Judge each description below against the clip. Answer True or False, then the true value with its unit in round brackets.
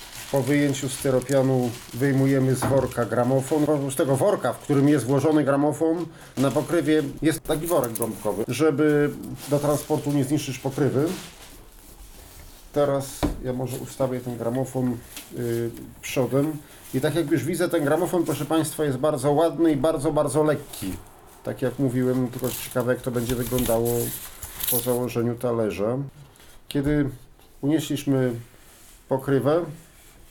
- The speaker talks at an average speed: True (135 wpm)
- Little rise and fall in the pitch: False (3.3 semitones)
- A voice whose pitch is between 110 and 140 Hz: True (135 Hz)